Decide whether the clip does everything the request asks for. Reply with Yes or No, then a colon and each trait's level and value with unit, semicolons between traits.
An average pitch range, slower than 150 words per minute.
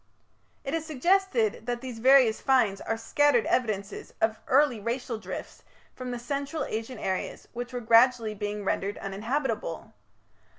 Yes: average, 3.5 semitones; average, 140 wpm